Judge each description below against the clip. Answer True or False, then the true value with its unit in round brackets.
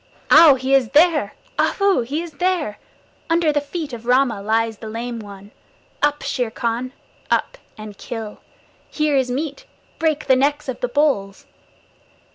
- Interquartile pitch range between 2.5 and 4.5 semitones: False (5.0 semitones)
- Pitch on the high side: True (265 Hz)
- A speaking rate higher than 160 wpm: False (155 wpm)